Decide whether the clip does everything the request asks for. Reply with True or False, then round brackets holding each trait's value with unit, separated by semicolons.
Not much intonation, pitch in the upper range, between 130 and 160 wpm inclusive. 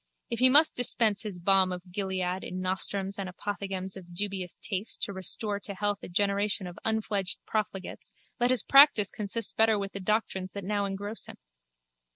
False (2.1 semitones; 200 Hz; 180 wpm)